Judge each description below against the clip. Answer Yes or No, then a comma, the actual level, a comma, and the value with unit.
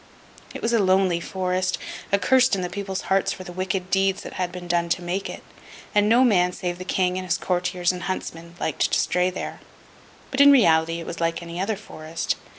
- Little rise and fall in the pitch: Yes, narrow, 1.8 semitones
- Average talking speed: No, fast, 215 wpm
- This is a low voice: No, medium, 185 Hz